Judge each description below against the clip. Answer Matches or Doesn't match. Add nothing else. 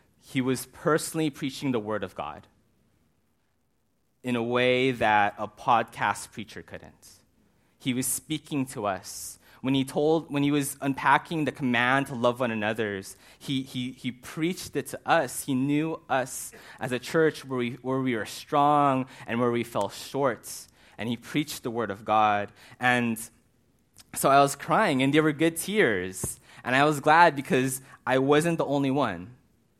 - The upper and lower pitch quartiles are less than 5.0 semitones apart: Matches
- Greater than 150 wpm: Matches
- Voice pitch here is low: Matches